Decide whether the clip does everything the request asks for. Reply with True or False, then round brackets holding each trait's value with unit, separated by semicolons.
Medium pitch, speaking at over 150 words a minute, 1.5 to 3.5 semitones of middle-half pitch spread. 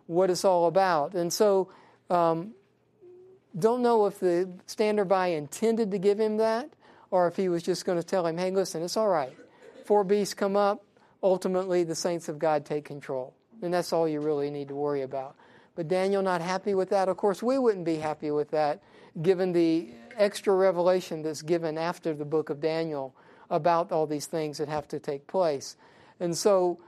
False (180 Hz; 195 wpm; 3.9 semitones)